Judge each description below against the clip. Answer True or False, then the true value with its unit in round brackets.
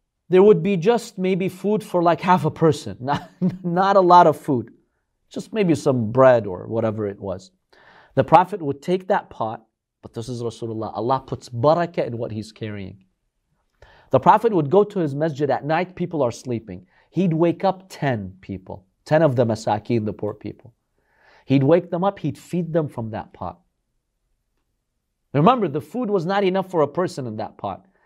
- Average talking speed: True (190 wpm)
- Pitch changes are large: True (8.3 semitones)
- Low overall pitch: False (150 Hz)